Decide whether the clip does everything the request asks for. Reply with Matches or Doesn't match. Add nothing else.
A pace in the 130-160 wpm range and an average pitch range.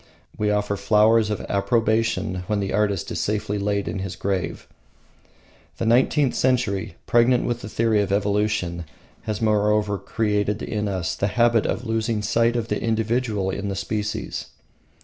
Doesn't match